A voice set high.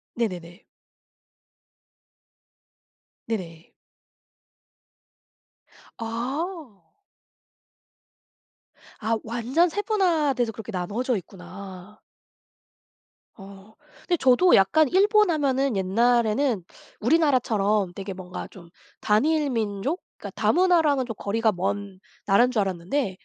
Yes: high, 225 Hz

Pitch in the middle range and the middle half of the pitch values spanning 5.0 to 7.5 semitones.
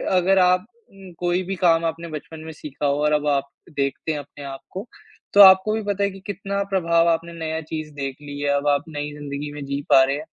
No: medium, 160 Hz; average, 4.1 semitones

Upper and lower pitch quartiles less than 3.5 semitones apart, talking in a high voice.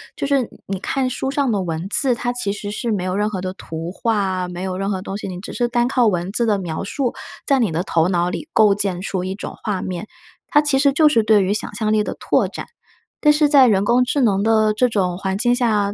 No: average, 4.5 semitones; high, 210 Hz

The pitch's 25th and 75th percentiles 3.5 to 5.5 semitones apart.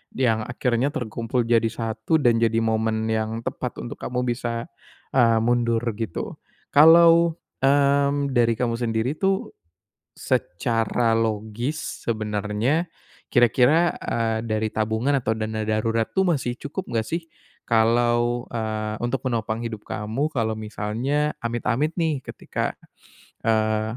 No: average, 2.9 semitones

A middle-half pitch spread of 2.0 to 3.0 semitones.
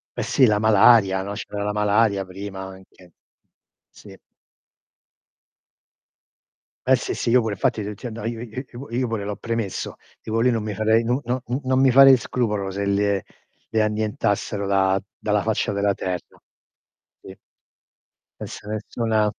Yes: narrow, 2.5 semitones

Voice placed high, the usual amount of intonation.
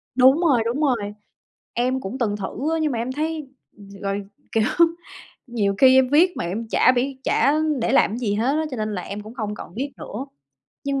Yes: high, 245 Hz; average, 4.6 semitones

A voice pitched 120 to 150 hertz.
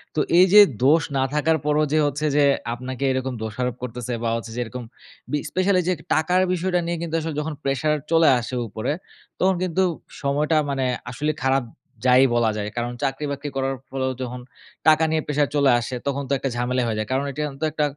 Yes: medium, 140 Hz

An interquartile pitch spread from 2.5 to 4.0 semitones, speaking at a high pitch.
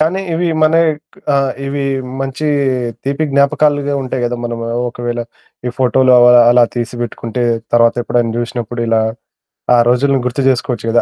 No: average, 2.8 semitones; low, 125 Hz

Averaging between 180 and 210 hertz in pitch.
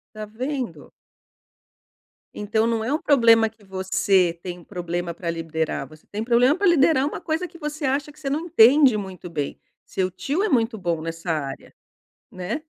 No: high, 220 Hz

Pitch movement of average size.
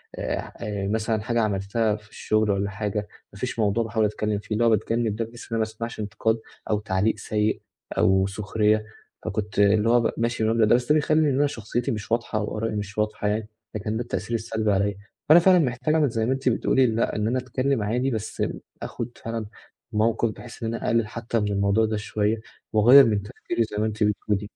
No: narrow, 2.0 semitones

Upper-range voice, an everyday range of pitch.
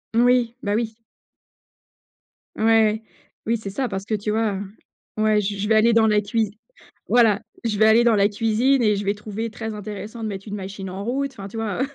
No: high, 215 Hz; narrow, 1.9 semitones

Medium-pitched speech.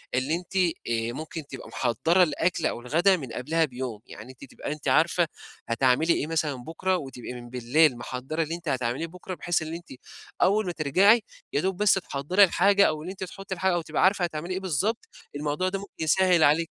Yes: medium, 160 Hz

